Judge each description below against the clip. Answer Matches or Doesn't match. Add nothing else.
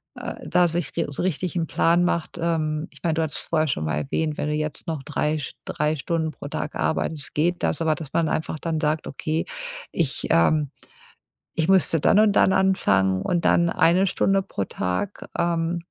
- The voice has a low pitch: Doesn't match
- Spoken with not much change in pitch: Matches